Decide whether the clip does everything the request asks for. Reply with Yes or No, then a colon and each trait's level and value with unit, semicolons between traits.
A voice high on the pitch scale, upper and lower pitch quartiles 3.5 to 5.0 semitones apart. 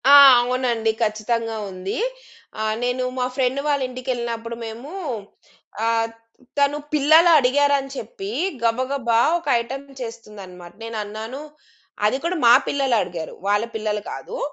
Yes: high, 235 Hz; average, 3.8 semitones